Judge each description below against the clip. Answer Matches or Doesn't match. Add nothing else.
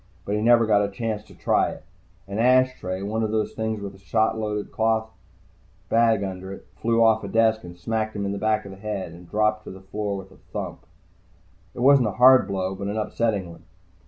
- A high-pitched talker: Doesn't match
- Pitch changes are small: Matches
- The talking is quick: Matches